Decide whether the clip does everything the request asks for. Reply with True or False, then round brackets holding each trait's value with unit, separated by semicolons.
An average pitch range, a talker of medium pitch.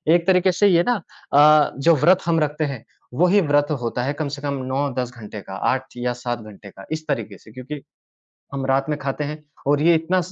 True (4.5 semitones; 145 Hz)